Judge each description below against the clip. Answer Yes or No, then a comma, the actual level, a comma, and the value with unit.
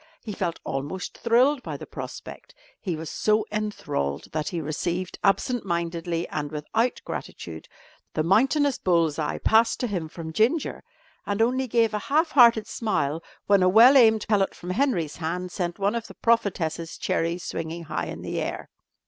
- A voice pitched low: No, high, 190 Hz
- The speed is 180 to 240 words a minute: No, average, 170 wpm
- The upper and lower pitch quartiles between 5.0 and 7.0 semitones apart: Yes, wide, 5.6 semitones